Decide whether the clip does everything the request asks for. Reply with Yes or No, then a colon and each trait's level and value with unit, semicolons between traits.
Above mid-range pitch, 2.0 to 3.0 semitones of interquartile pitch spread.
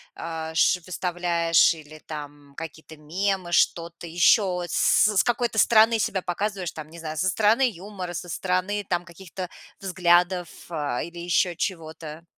No: medium, 175 Hz; average, 2.7 semitones